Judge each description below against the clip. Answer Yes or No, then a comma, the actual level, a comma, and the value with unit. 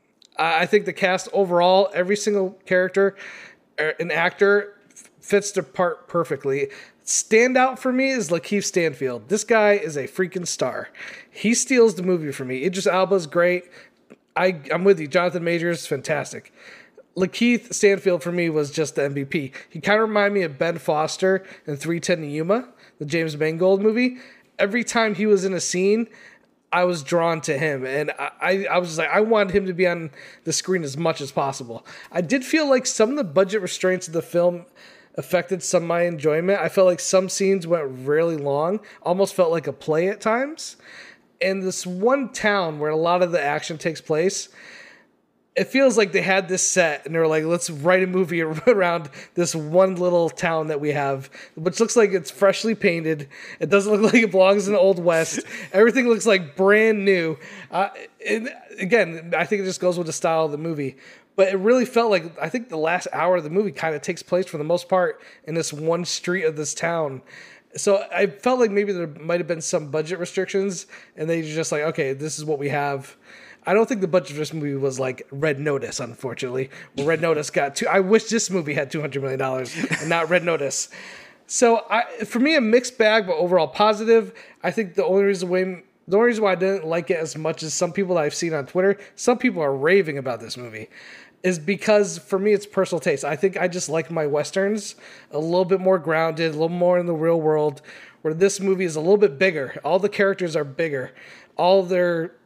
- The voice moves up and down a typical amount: Yes, average, 3.8 semitones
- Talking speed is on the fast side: Yes, fast, 210 wpm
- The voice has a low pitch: No, medium, 180 Hz